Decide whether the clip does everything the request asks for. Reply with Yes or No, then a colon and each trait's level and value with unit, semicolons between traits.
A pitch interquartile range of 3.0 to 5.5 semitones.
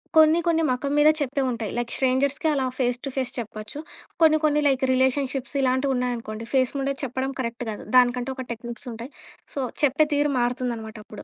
No: narrow, 2.6 semitones